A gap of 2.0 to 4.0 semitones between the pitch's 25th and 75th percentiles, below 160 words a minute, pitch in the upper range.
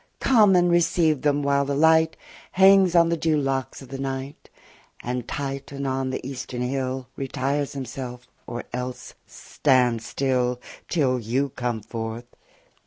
No: average, 3.0 semitones; average, 150 wpm; low, 135 Hz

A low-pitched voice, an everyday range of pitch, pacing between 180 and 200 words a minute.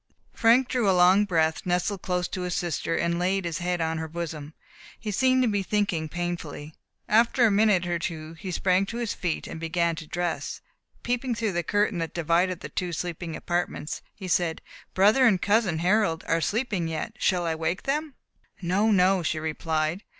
No: medium, 180 Hz; average, 3.8 semitones; average, 190 wpm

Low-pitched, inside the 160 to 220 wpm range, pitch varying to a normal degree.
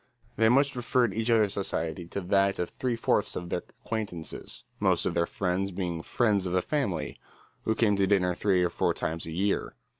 Yes: very low, 95 Hz; average, 200 wpm; average, 4.0 semitones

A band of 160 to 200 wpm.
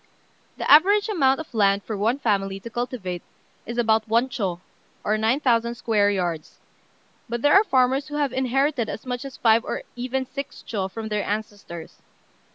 Yes: average, 170 wpm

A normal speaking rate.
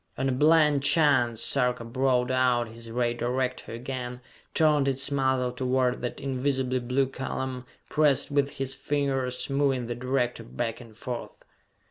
Yes: average, 145 wpm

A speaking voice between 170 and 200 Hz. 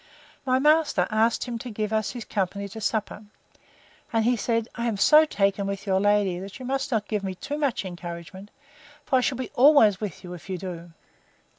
No: high, 210 Hz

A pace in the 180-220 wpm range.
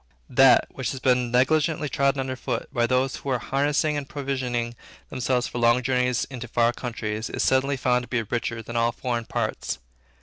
Yes: average, 190 wpm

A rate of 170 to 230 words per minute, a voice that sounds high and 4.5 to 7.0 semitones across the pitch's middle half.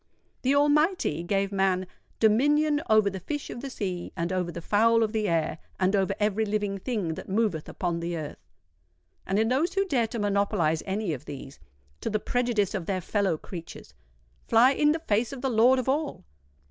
Yes: average, 190 wpm; high, 210 Hz; average, 5.1 semitones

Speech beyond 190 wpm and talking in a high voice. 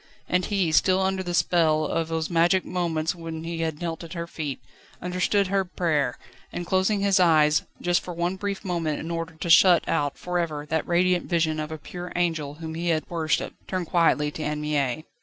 No: fast, 205 wpm; medium, 170 Hz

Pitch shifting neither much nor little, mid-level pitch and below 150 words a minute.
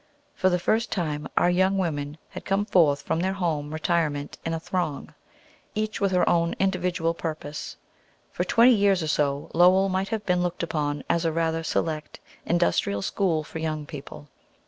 No: average, 3.5 semitones; medium, 170 Hz; average, 175 wpm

